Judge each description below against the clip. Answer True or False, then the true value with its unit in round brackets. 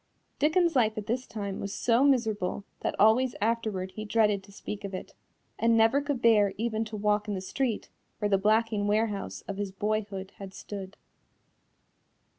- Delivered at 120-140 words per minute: False (175 wpm)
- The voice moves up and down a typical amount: False (2.3 semitones)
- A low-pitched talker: False (215 Hz)